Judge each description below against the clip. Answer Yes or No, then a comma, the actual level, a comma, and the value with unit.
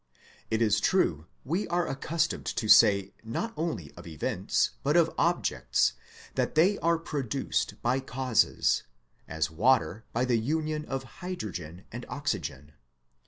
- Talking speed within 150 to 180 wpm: No, slow, 135 wpm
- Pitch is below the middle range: Yes, low, 120 Hz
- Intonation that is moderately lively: No, wide, 8.5 semitones